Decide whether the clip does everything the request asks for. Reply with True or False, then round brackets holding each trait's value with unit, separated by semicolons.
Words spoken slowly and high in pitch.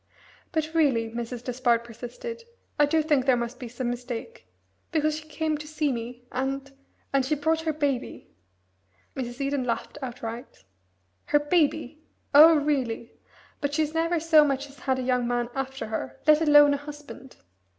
False (165 wpm; 275 Hz)